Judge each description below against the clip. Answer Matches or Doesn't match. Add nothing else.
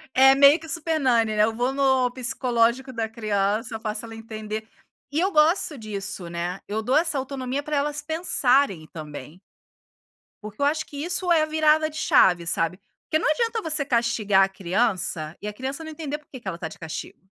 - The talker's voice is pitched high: Matches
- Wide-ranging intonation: Matches